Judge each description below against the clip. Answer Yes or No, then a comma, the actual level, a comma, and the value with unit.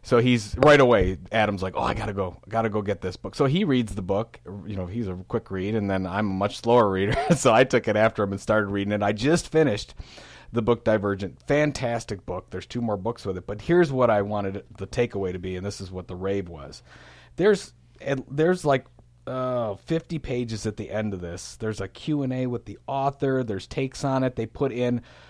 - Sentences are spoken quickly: Yes, fast, 235 wpm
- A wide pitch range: No, average, 4.4 semitones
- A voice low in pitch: Yes, low, 110 Hz